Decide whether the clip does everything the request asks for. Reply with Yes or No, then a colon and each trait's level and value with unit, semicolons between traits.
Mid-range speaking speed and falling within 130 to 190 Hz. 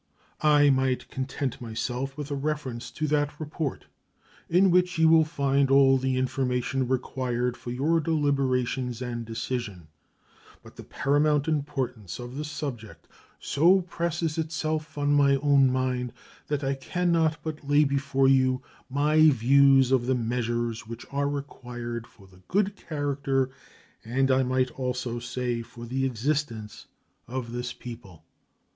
Yes: average, 145 wpm; low, 135 Hz